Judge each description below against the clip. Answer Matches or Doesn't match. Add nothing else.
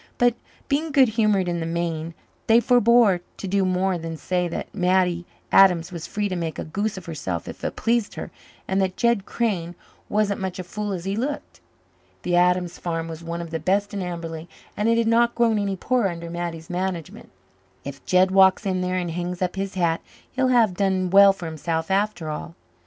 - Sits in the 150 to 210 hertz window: Matches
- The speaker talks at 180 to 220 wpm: Matches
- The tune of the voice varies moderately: Matches